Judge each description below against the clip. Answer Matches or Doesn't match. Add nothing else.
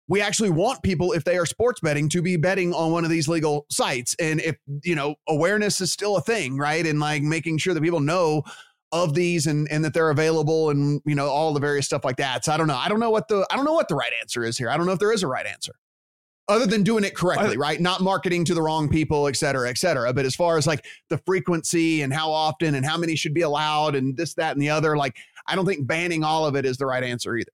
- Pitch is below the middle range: Doesn't match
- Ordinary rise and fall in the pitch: Matches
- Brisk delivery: Matches